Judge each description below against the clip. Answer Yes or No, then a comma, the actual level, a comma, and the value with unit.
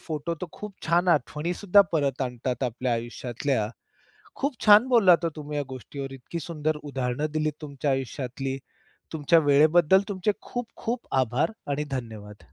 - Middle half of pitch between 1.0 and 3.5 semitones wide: No, average, 4.8 semitones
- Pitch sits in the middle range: Yes, medium, 145 Hz